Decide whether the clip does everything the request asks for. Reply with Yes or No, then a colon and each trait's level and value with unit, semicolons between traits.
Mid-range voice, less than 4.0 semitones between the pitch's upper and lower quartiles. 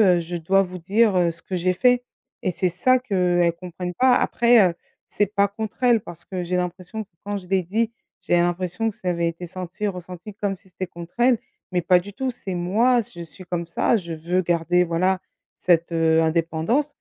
Yes: medium, 180 Hz; average, 3.1 semitones